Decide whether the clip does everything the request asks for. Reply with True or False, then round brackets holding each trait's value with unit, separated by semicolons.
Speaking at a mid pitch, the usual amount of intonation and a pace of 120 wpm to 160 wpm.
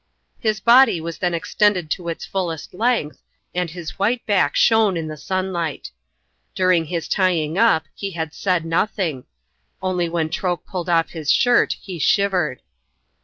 True (180 Hz; 3.2 semitones; 155 wpm)